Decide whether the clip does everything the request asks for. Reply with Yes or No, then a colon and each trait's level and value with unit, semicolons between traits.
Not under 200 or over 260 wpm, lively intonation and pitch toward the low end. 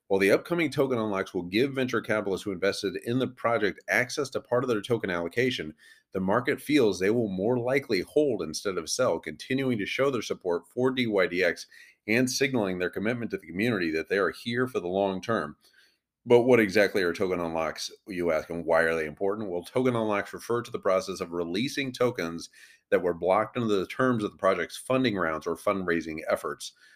Yes: fast, 205 wpm; wide, 5.8 semitones; low, 105 Hz